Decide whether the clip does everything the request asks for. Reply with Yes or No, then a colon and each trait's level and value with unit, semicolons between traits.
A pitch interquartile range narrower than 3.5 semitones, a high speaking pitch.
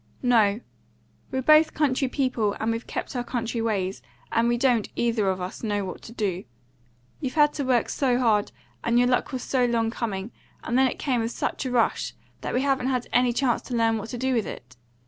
Yes: narrow, 2.6 semitones; high, 240 Hz